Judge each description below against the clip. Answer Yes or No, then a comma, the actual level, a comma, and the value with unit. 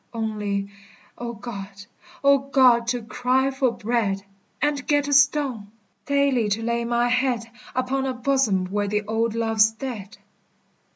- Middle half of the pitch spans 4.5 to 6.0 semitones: No, average, 3.9 semitones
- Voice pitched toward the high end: Yes, high, 235 Hz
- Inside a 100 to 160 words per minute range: Yes, average, 140 wpm